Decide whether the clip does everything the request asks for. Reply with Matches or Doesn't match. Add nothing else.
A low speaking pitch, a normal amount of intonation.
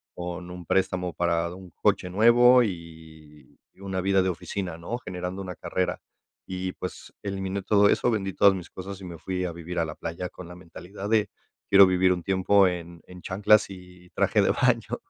Doesn't match